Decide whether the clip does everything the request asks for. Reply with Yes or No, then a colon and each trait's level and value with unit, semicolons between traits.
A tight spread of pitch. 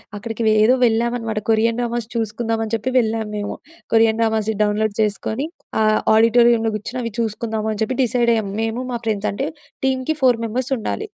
Yes: narrow, 1.6 semitones